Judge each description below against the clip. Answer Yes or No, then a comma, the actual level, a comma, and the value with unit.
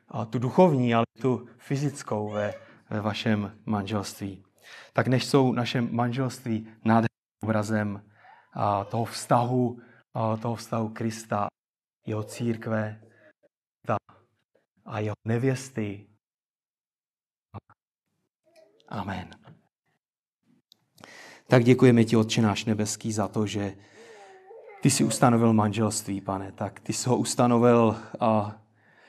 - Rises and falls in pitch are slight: Yes, narrow, 2.3 semitones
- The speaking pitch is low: Yes, low, 115 Hz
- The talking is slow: Yes, slow, 105 wpm